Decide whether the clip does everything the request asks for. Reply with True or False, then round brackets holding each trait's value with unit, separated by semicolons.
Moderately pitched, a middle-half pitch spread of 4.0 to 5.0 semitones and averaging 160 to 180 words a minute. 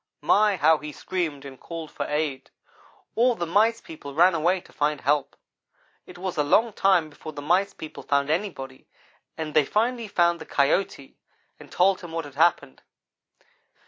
True (165 Hz; 4.4 semitones; 175 wpm)